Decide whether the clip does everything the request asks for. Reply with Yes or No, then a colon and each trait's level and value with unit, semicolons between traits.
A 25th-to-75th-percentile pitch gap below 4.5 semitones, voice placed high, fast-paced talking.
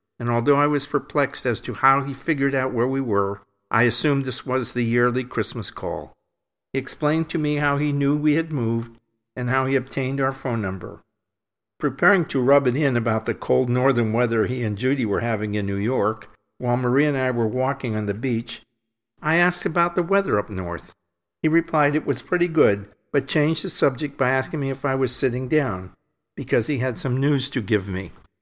No: average, 4.1 semitones; low, 130 Hz; fast, 210 wpm